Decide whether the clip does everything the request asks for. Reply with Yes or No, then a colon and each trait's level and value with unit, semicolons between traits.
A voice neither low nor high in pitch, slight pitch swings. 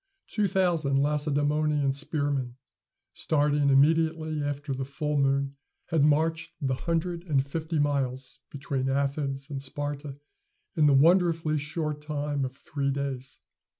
Yes: medium, 145 Hz; narrow, 2.0 semitones